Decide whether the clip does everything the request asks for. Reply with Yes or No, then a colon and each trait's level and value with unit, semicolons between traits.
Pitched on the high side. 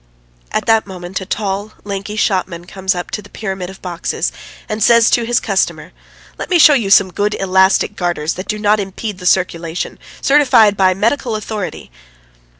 Yes: high, 195 Hz